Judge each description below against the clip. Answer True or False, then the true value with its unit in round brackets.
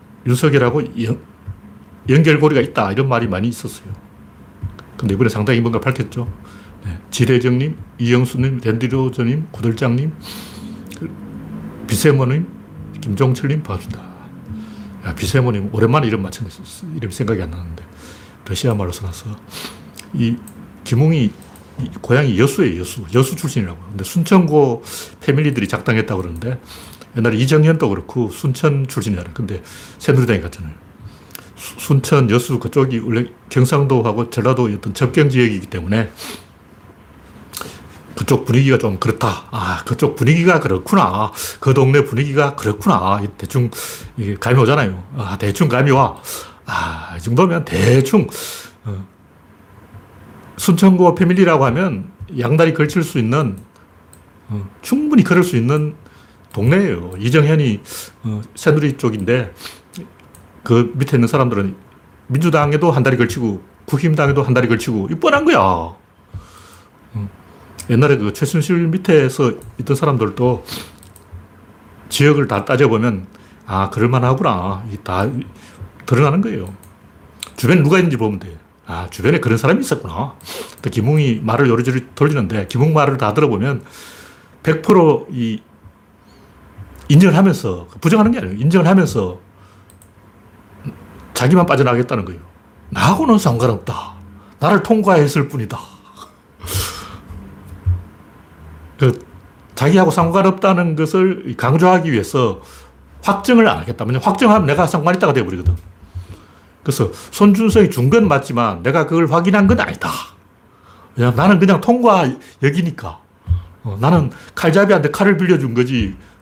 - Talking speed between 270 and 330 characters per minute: True (290 characters per minute)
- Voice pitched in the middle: False (120 Hz)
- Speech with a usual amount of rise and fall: False (6.7 semitones)